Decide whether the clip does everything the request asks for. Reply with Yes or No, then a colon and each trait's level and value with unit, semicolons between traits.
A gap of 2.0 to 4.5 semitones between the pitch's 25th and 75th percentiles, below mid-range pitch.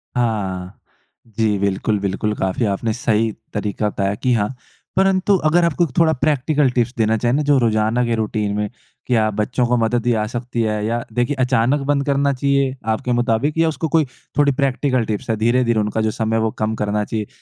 Yes: average, 3.8 semitones; low, 115 Hz